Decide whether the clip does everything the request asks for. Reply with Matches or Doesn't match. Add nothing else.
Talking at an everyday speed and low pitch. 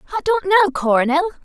Doesn't match